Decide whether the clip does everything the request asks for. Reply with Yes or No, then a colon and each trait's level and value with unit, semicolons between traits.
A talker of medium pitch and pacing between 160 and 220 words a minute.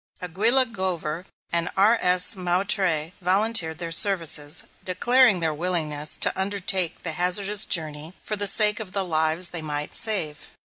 No: medium, 180 Hz; average, 140 wpm